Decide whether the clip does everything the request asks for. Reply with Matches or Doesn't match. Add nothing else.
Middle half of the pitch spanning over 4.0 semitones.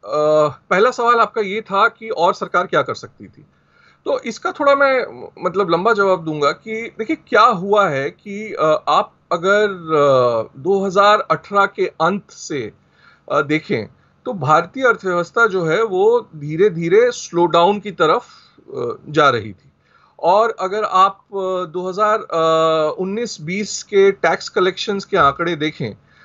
Matches